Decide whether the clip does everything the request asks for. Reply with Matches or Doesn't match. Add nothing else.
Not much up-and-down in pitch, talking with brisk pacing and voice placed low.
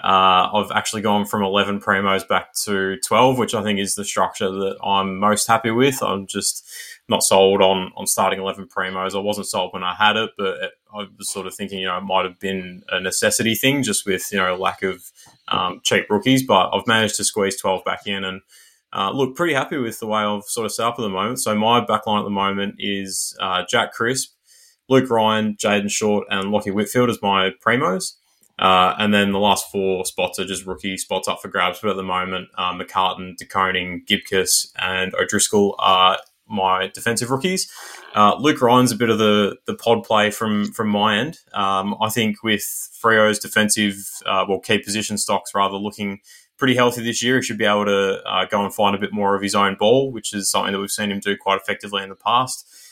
Matches